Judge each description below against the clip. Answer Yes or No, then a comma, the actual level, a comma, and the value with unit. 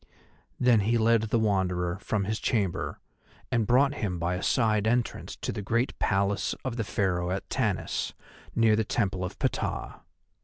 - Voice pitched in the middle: No, low, 105 Hz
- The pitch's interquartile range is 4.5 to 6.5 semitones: No, average, 3.3 semitones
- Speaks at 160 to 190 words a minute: Yes, average, 165 wpm